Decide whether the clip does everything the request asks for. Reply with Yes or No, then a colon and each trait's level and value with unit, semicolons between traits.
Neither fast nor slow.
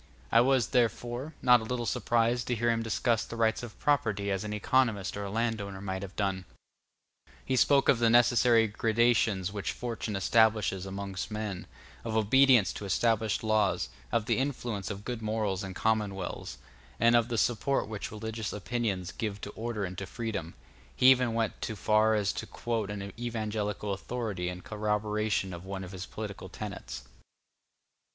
Yes: average, 170 wpm